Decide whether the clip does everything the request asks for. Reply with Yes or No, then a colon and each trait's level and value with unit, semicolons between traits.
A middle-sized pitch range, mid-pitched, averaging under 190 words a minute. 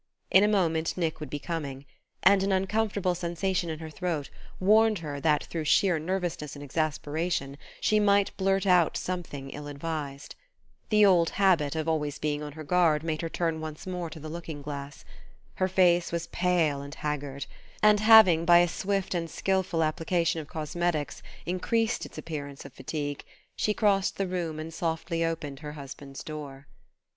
Yes: average, 3.6 semitones; medium, 165 Hz; average, 170 wpm